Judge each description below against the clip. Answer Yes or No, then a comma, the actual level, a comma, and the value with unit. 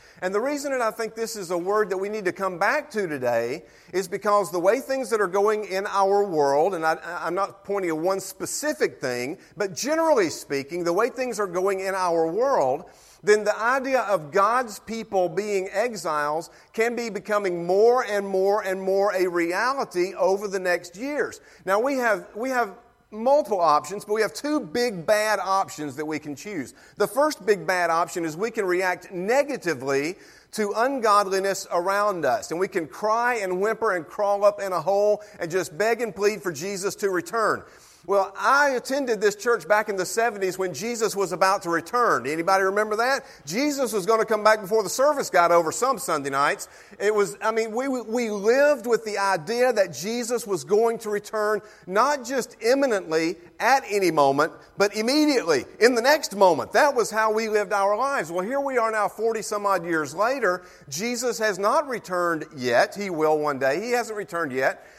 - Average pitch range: Yes, average, 3.9 semitones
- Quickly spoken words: No, average, 195 wpm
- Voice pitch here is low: No, high, 205 Hz